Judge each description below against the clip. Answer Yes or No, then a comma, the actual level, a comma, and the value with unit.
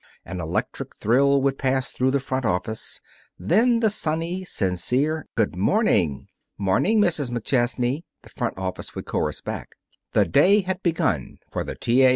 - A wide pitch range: Yes, wide, 7.4 semitones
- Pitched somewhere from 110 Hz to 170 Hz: Yes, low, 135 Hz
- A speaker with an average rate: Yes, average, 160 wpm